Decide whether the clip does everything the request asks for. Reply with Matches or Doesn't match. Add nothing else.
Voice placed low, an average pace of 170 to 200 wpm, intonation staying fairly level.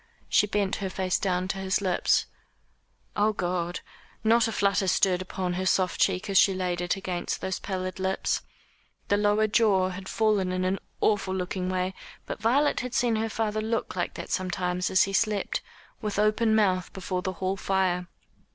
Doesn't match